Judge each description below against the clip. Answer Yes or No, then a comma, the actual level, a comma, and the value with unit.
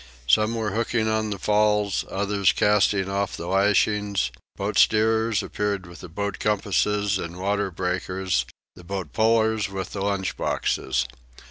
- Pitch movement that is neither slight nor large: No, narrow, 1.9 semitones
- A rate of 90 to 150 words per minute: Yes, average, 140 wpm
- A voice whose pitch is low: Yes, low, 100 Hz